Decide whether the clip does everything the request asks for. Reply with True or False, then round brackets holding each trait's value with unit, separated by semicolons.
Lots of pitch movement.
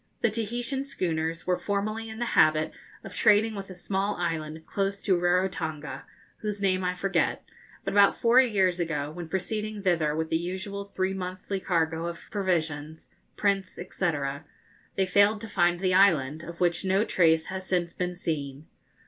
False (3.4 semitones)